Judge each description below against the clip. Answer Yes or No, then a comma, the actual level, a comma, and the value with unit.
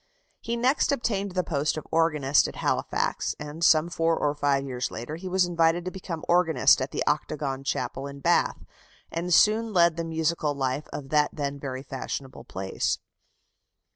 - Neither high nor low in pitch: Yes, medium, 155 Hz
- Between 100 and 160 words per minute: No, average, 170 wpm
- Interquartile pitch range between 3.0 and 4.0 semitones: Yes, average, 3.7 semitones